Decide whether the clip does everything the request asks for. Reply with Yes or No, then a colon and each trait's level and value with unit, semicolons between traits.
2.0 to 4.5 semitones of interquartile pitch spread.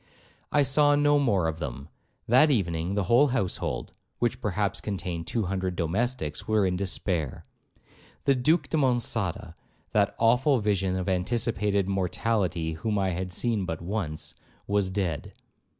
No: average, 5.1 semitones